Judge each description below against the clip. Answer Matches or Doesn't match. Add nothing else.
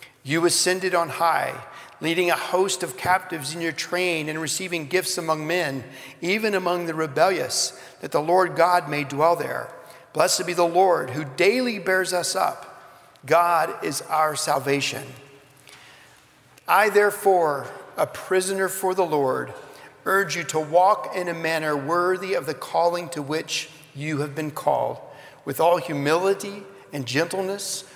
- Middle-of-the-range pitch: Matches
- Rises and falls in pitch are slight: Doesn't match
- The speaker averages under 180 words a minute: Matches